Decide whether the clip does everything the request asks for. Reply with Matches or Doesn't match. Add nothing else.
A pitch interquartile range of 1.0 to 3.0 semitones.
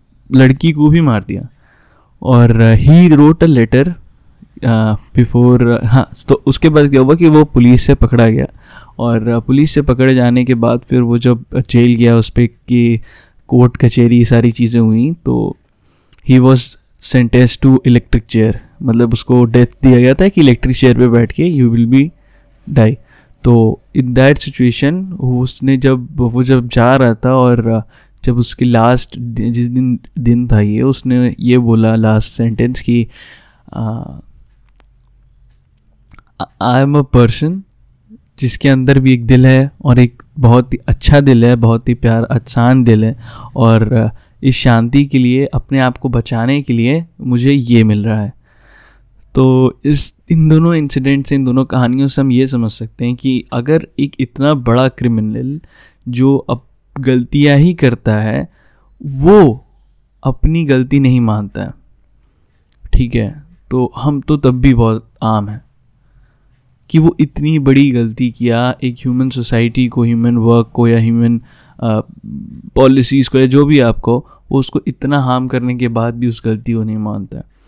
Matches